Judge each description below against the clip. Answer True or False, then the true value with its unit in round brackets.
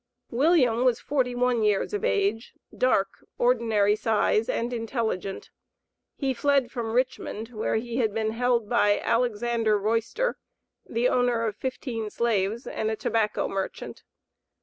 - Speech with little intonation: True (2.3 semitones)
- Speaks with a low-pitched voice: False (230 Hz)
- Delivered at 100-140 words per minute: True (135 wpm)